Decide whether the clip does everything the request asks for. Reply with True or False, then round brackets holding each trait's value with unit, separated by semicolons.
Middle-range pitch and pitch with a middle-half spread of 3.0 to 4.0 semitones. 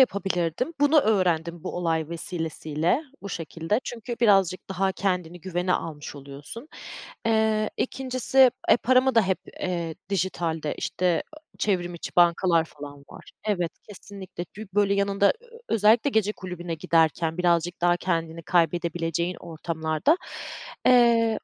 False (180 Hz; 4.4 semitones)